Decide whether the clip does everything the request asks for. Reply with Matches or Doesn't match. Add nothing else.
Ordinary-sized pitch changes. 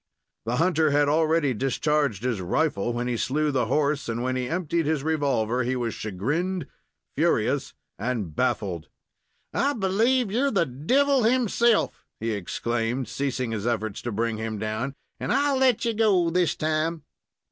Doesn't match